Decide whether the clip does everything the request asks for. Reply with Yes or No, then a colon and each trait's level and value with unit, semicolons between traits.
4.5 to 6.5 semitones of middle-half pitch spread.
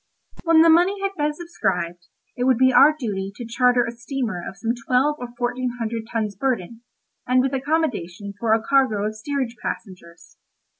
No: average, 4.1 semitones